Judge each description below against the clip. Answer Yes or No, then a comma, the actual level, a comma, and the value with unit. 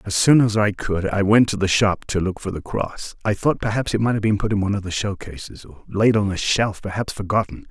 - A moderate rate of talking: No, fast, 275 wpm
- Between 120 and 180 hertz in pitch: No, low, 100 Hz